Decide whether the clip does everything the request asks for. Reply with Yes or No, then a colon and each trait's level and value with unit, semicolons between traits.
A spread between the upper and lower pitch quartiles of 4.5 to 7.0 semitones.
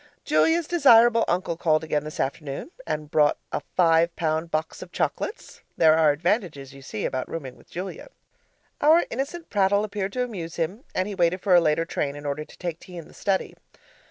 Yes: average, 4.9 semitones